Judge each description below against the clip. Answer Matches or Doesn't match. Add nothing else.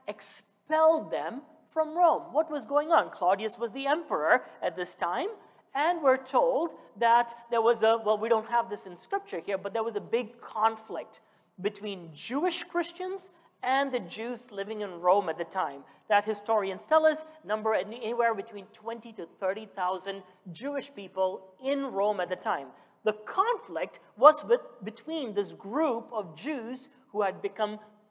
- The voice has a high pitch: Matches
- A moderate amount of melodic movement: Doesn't match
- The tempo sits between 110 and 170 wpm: Matches